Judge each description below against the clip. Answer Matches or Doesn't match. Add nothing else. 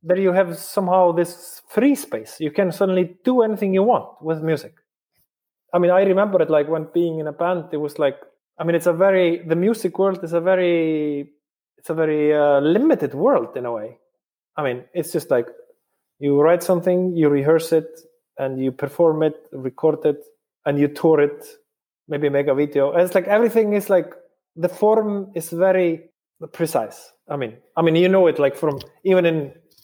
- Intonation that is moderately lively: Matches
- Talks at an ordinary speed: Matches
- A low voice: Doesn't match